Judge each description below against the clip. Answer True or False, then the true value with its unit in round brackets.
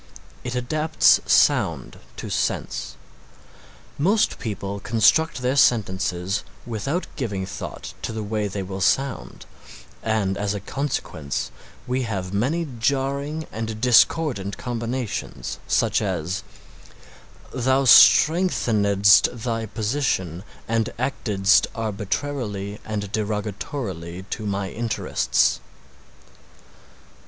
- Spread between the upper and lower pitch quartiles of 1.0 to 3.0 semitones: False (4.6 semitones)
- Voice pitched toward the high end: False (110 Hz)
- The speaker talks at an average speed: False (95 wpm)